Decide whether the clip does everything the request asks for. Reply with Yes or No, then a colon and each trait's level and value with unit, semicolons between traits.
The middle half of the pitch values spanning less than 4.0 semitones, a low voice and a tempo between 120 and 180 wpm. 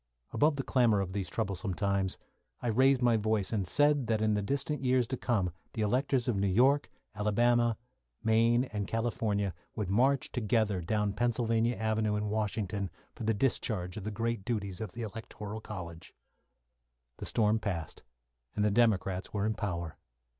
Yes: average, 2.9 semitones; low, 110 Hz; average, 170 wpm